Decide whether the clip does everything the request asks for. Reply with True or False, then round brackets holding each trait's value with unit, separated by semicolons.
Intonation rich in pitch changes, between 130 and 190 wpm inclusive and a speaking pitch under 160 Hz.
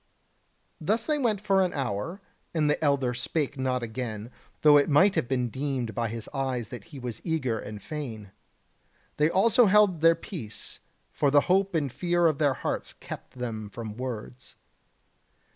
True (5.7 semitones; 170 wpm; 140 Hz)